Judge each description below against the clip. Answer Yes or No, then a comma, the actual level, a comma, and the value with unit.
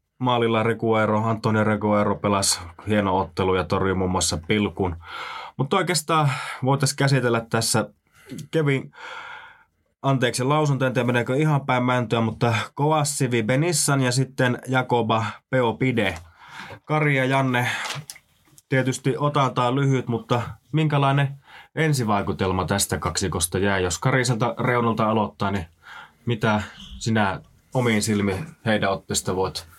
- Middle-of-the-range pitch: No, low, 120 Hz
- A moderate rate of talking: Yes, average, 115 wpm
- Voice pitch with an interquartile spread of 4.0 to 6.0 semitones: Yes, average, 4.6 semitones